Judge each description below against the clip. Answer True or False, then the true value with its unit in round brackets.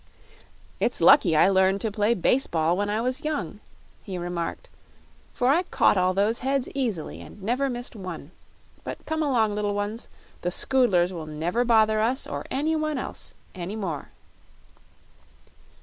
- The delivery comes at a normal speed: True (155 wpm)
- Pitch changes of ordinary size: False (5.7 semitones)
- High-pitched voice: True (210 Hz)